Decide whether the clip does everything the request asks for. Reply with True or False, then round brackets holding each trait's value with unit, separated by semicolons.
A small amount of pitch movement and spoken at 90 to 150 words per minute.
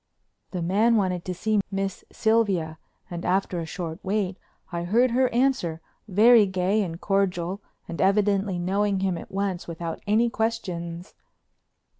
False (3.3 semitones; 145 wpm)